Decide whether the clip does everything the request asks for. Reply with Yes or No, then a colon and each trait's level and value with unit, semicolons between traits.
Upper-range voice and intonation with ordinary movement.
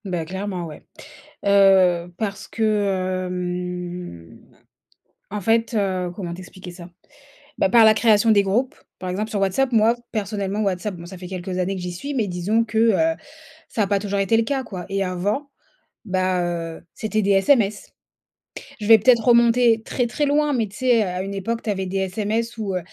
Yes: high, 200 Hz; average, 3.7 semitones